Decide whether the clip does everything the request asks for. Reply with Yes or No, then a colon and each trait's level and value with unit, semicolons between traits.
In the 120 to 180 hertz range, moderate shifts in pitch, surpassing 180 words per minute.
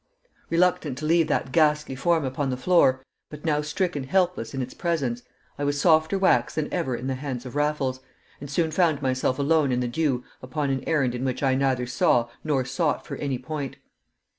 Yes: medium, 140 Hz; average, 3.5 semitones; average, 200 wpm